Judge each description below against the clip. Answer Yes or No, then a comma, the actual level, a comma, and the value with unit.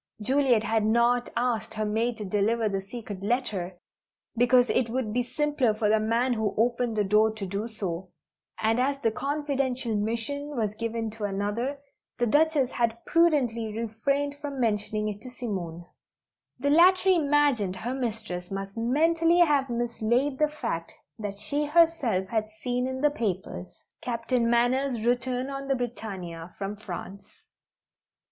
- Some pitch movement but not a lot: Yes, average, 3.9 semitones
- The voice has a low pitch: No, high, 235 Hz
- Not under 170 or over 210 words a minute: No, average, 155 wpm